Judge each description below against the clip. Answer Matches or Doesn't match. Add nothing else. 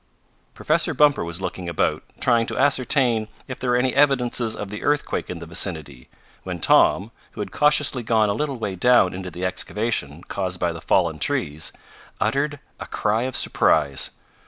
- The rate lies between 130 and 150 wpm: Doesn't match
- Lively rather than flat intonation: Matches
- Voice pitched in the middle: Doesn't match